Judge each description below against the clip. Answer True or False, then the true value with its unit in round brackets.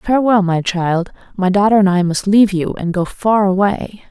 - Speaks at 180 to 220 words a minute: True (205 wpm)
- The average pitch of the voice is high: True (195 Hz)